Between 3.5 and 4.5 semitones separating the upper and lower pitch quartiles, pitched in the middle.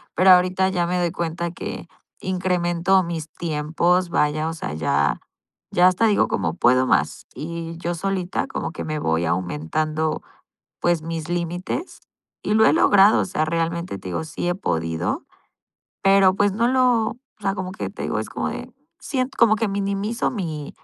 Yes: average, 3.8 semitones; medium, 175 Hz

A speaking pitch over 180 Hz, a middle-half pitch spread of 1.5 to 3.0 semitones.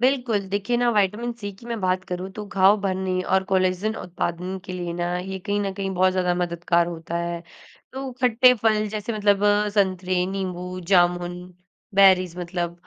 Yes: high, 190 Hz; narrow, 2.5 semitones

